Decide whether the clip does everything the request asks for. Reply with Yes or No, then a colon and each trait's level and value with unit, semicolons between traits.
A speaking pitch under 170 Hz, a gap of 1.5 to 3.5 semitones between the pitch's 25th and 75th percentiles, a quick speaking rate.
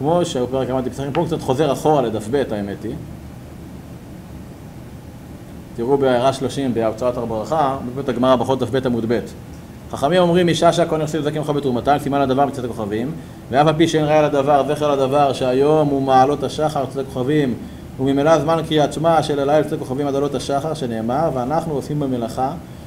Yes: medium, 140 Hz; average, 3.1 semitones; fast, 165 wpm